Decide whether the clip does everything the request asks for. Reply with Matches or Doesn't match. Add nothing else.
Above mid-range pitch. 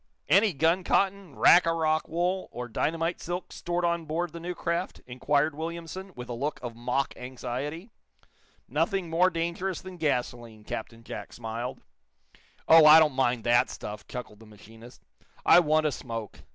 Doesn't match